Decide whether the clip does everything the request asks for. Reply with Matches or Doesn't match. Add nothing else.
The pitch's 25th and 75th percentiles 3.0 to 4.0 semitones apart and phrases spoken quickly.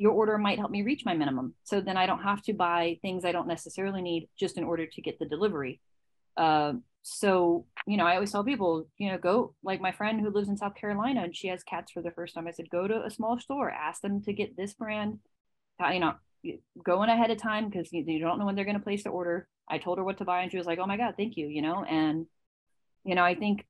Matches